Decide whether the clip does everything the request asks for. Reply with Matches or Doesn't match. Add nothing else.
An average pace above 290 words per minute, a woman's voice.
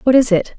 Matches